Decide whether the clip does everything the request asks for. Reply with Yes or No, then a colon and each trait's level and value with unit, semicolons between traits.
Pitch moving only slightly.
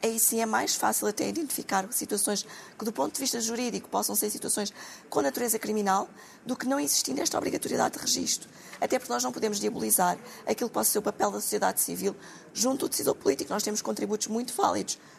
No: average, 3.8 semitones